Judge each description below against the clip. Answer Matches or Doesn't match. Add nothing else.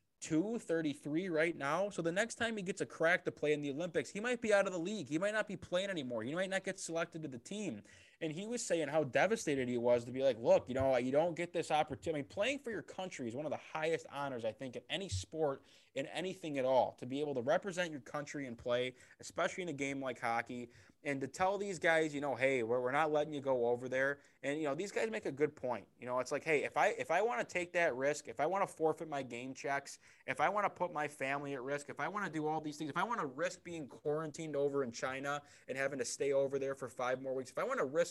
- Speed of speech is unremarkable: Doesn't match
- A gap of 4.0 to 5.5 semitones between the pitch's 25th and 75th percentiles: Matches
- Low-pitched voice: Doesn't match